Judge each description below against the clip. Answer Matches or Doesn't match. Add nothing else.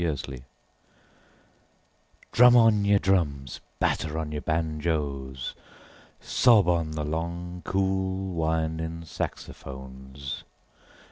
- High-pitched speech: Doesn't match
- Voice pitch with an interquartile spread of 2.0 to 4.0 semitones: Doesn't match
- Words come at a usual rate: Doesn't match